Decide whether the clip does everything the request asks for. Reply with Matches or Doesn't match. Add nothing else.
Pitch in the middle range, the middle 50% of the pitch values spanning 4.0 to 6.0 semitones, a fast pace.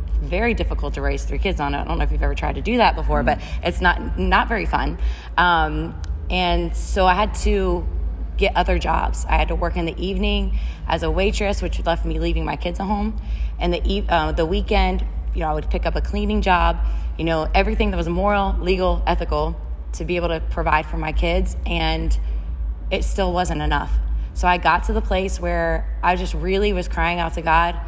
Matches